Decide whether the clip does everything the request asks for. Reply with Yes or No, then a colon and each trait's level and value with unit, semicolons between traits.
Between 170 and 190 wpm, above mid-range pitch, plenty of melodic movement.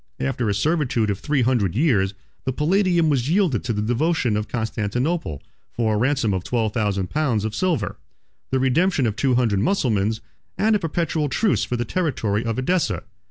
No: average, 180 wpm; low, 125 Hz; wide, 6.5 semitones